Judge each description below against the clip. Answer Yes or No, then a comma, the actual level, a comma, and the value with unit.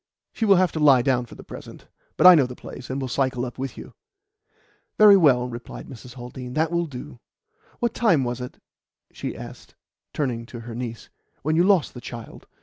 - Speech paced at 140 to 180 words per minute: No, fast, 205 wpm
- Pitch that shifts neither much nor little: Yes, average, 4.6 semitones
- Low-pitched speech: Yes, low, 130 Hz